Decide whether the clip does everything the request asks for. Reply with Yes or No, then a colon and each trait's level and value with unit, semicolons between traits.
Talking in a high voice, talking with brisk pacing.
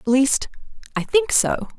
No: very high, 285 Hz; average, 170 wpm